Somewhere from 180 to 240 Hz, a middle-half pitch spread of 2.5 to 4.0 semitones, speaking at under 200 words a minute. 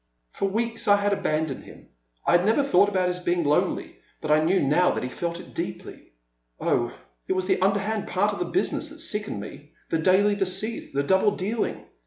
No: high, 190 Hz; average, 3.3 semitones; fast, 205 wpm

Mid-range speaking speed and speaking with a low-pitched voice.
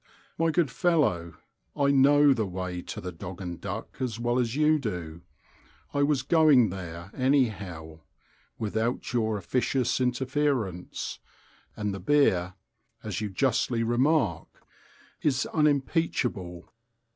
No: slow, 120 wpm; low, 120 Hz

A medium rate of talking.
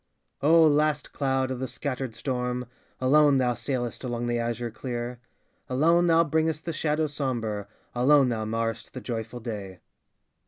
Yes: average, 150 wpm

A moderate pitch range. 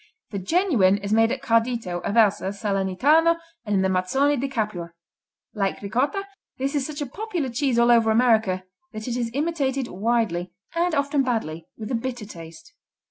No: wide, 5.7 semitones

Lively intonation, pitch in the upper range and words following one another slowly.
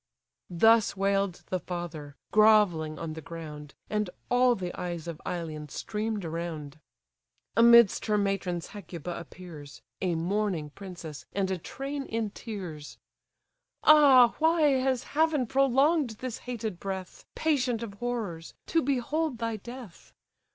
Yes: wide, 6.3 semitones; high, 200 Hz; slow, 130 wpm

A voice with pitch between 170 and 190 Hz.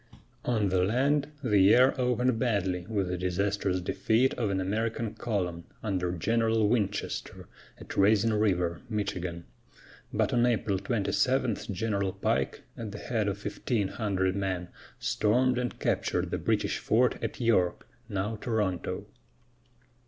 No: low, 105 Hz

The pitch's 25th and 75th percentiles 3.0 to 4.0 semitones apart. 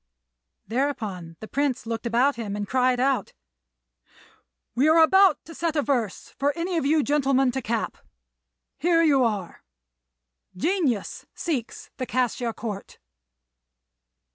No: average, 4.4 semitones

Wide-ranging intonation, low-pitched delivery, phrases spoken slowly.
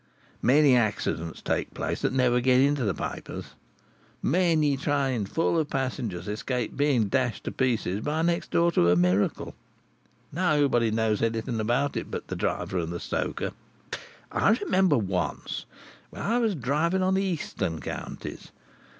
No: wide, 6.0 semitones; low, 130 Hz; average, 150 wpm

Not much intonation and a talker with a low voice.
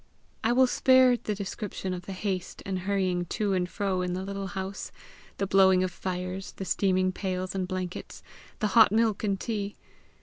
No: narrow, 1.8 semitones; high, 190 Hz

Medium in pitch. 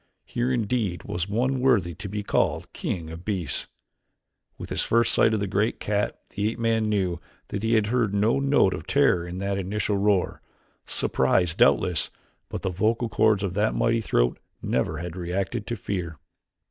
No: low, 100 Hz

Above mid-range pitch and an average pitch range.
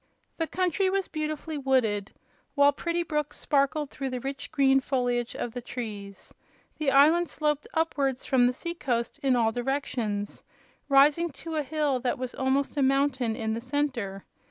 Yes: very high, 275 Hz; average, 3.5 semitones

